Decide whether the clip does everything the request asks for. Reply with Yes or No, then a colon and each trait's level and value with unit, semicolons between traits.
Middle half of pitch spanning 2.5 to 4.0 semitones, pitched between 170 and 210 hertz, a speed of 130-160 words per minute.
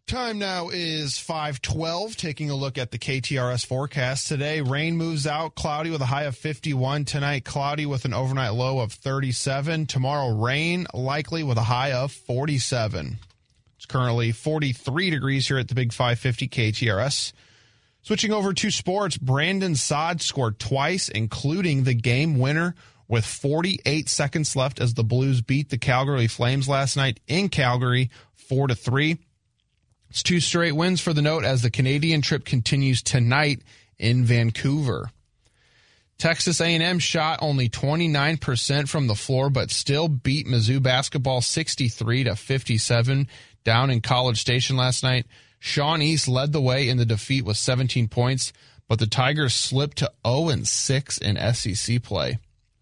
No: average, 3.7 semitones; low, 135 Hz; average, 150 wpm